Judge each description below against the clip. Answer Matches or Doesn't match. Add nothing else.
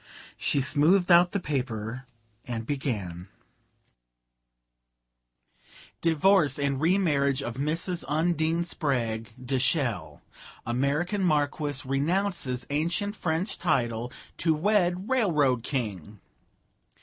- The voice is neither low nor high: Matches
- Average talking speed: Doesn't match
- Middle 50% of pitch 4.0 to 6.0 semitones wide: Matches